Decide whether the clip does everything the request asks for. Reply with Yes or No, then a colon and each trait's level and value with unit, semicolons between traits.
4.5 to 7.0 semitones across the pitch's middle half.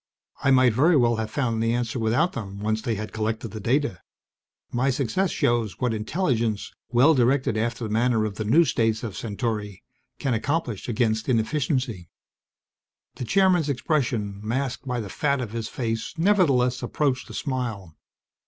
No: average, 3.6 semitones